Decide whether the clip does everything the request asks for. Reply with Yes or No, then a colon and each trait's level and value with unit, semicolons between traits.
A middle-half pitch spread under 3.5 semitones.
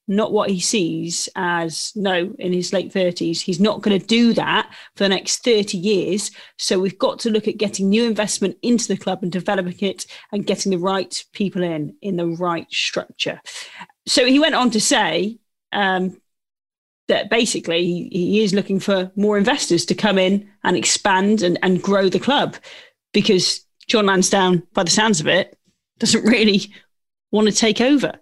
Yes: narrow, 2.6 semitones